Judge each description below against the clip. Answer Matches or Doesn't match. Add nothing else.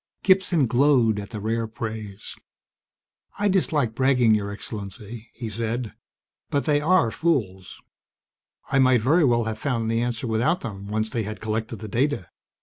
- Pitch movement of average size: Matches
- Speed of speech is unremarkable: Matches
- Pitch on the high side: Doesn't match